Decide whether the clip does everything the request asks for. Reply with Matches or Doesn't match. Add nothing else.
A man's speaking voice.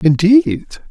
Matches